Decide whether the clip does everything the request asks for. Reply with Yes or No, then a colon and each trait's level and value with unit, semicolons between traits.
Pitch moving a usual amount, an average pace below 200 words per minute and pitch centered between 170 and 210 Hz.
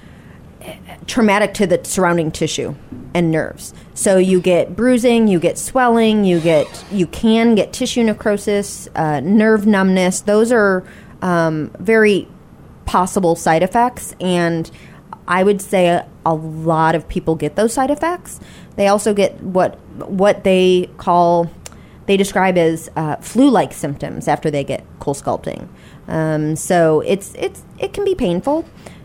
Yes: average, 4.3 semitones; average, 145 wpm; medium, 185 Hz